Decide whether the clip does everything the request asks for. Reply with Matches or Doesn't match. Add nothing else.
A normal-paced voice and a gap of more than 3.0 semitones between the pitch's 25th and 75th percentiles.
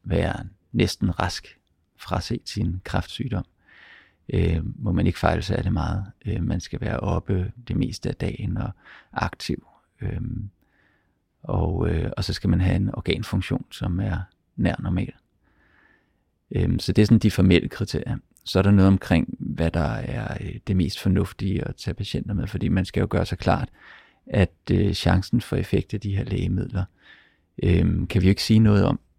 Doesn't match